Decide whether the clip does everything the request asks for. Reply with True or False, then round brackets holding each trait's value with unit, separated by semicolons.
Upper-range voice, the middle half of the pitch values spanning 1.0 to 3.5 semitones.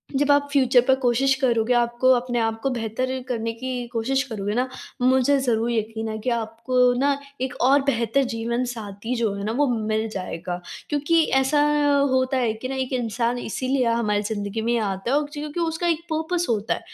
True (245 Hz; 3.0 semitones)